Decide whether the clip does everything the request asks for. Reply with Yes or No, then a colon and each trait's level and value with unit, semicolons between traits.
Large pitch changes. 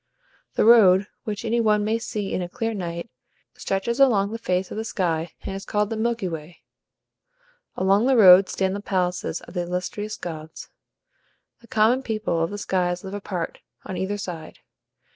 No: average, 3.3 semitones